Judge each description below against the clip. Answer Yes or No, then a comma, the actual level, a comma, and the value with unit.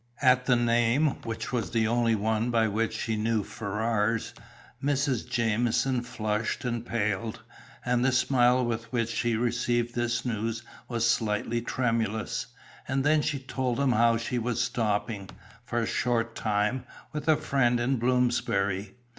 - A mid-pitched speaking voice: No, low, 120 Hz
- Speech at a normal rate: Yes, average, 150 wpm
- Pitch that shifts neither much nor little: No, narrow, 1.8 semitones